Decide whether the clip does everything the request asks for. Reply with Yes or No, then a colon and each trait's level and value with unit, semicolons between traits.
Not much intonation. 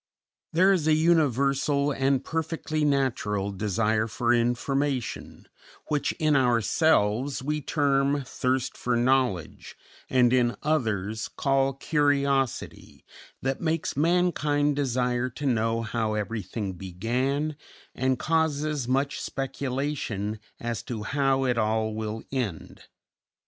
No: average, 4.1 semitones